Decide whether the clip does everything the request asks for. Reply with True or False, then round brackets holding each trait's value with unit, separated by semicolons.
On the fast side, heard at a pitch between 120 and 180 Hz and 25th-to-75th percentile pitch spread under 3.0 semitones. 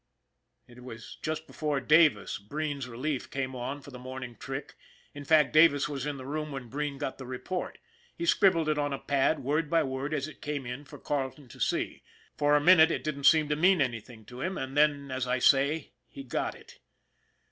True (210 wpm; 140 Hz; 2.6 semitones)